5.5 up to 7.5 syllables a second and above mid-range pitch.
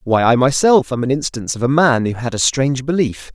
No: 5.9 syllables/s; low, 130 Hz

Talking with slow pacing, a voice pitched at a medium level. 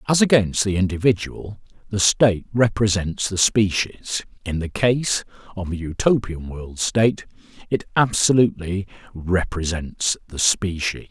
No: slow, 120 wpm; low, 100 Hz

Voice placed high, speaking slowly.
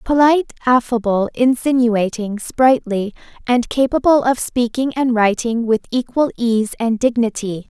Yes: high, 240 Hz; slow, 115 wpm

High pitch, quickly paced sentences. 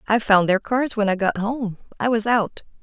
Yes: high, 215 Hz; fast, 235 wpm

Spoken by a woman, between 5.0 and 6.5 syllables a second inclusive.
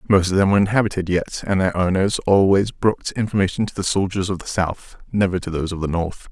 No: male; 6.0 syllables/s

